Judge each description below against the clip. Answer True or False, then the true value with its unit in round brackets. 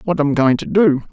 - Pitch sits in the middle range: True (155 Hz)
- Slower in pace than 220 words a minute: False (270 wpm)